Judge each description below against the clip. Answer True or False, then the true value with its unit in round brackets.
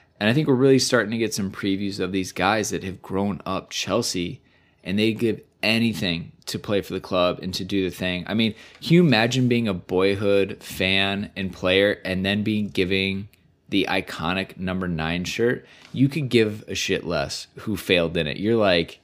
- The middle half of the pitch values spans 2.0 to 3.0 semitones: False (3.4 semitones)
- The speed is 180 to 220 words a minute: True (200 wpm)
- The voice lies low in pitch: True (100 Hz)